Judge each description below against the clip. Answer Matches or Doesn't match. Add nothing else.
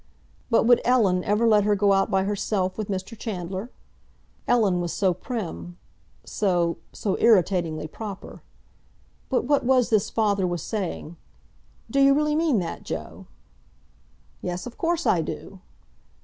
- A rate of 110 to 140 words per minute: Matches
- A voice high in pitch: Matches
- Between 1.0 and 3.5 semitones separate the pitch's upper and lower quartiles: Doesn't match